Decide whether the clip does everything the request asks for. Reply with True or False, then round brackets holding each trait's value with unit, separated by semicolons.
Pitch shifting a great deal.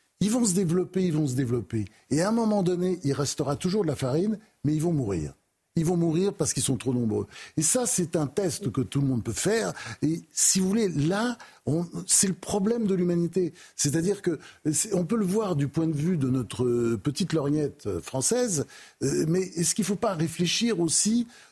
True (5.7 semitones)